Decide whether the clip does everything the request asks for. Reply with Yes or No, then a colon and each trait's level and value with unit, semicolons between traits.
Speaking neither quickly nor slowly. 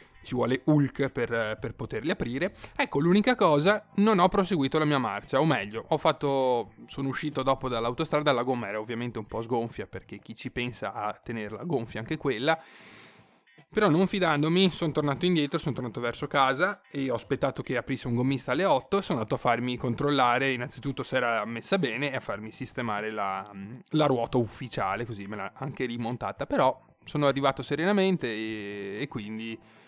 No: fast, 180 wpm